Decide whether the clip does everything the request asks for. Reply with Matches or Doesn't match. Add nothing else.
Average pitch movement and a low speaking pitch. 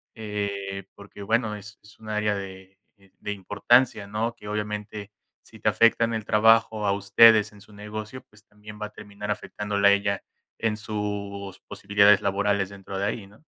Doesn't match